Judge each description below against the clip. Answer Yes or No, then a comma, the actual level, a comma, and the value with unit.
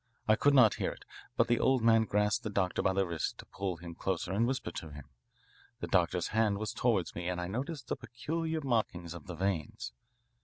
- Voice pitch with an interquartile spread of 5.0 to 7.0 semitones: Yes, average, 5.3 semitones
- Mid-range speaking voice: No, low, 100 Hz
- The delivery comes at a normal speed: No, fast, 220 wpm